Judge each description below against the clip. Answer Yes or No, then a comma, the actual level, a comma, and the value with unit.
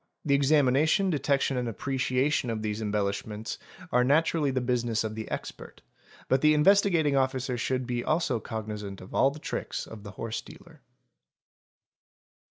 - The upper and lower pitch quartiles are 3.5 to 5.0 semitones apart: Yes, average, 4.5 semitones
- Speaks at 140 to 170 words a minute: Yes, average, 160 wpm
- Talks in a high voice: No, low, 125 Hz